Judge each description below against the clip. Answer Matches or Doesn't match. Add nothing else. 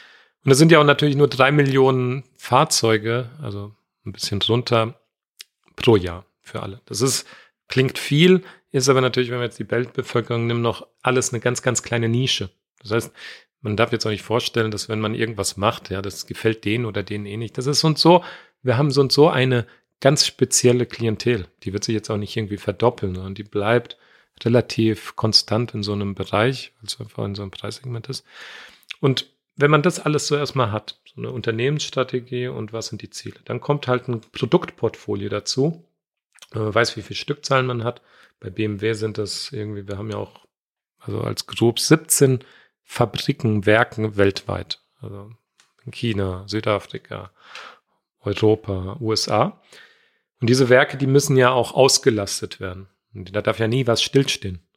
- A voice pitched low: Matches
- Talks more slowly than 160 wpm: Doesn't match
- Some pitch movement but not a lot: Matches